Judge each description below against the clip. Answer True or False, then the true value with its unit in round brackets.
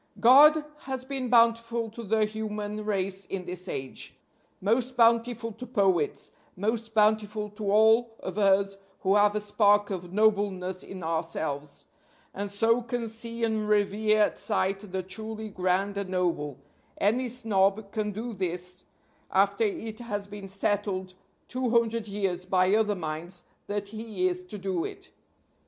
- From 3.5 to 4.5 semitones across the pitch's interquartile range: False (2.9 semitones)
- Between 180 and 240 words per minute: False (150 wpm)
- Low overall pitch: False (205 Hz)